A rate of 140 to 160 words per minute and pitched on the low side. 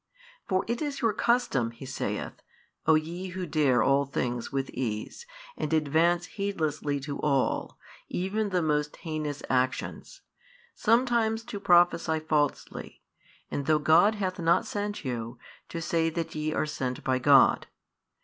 No: average, 145 wpm; medium, 160 Hz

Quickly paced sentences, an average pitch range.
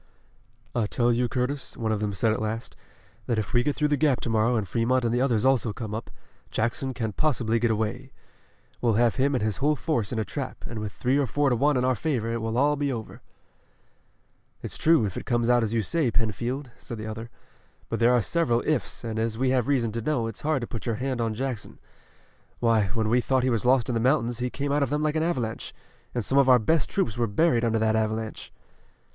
Yes: fast, 245 wpm; average, 3.1 semitones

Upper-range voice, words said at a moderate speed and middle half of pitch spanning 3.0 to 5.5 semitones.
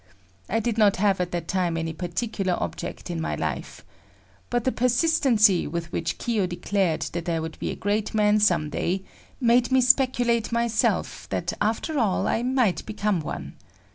Yes: high, 210 Hz; average, 170 wpm; average, 5.1 semitones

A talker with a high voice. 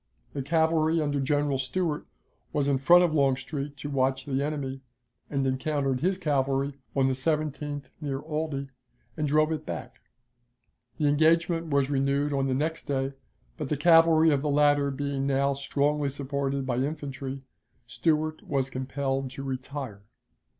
No: medium, 140 Hz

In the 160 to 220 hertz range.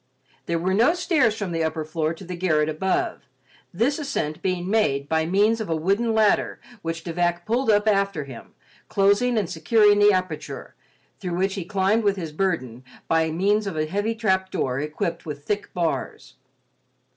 Yes: medium, 185 Hz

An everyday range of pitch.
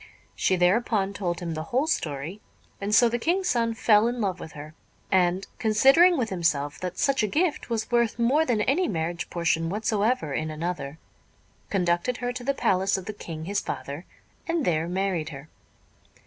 No: wide, 6.0 semitones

